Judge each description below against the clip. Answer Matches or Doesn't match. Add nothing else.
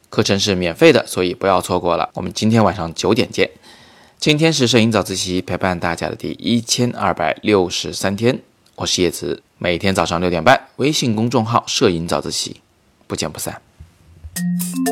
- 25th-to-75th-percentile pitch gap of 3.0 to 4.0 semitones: Doesn't match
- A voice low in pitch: Matches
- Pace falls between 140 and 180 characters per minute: Doesn't match